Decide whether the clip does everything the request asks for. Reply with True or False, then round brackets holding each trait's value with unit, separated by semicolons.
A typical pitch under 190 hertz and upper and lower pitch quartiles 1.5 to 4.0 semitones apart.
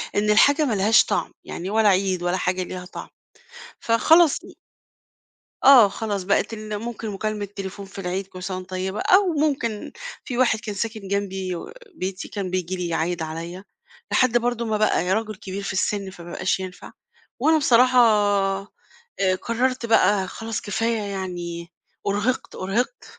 False (200 Hz; 3.5 semitones)